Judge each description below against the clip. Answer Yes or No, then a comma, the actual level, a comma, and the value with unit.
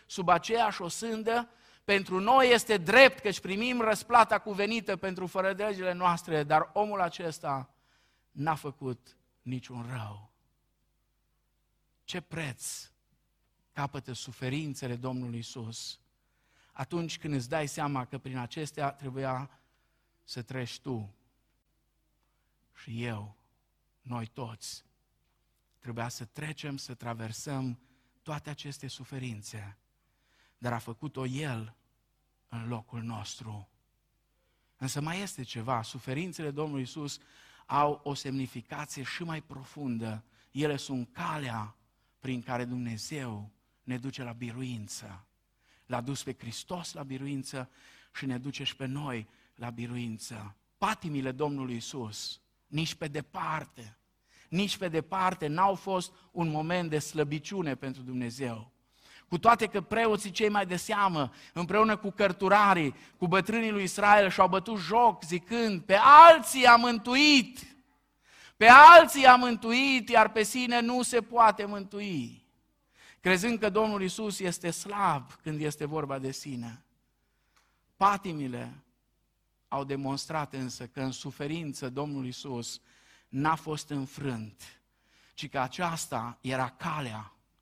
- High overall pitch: No, medium, 140 Hz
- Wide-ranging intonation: Yes, wide, 7.0 semitones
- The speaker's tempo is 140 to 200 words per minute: No, average, 120 wpm